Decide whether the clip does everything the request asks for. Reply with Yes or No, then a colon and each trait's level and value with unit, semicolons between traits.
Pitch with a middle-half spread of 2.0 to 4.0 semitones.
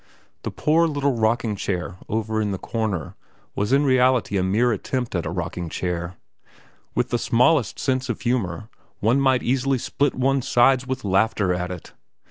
No: average, 5.1 semitones